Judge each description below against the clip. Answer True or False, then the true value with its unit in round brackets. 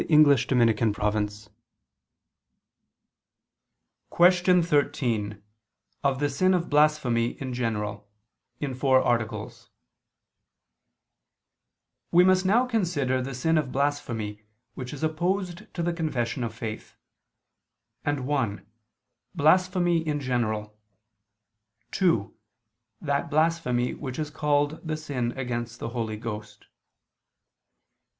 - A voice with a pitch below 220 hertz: True (135 Hz)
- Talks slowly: True (100 wpm)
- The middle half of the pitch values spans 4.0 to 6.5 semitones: True (5.4 semitones)